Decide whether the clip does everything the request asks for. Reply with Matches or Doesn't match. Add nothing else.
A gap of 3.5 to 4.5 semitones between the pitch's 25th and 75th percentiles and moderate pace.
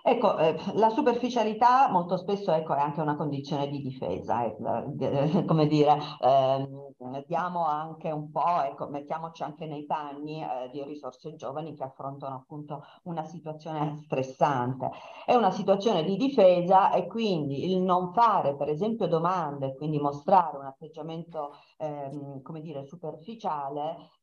Matches